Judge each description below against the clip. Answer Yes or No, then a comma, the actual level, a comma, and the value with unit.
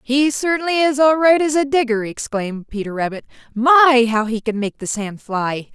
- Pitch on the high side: Yes, very high, 250 Hz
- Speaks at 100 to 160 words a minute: No, average, 200 wpm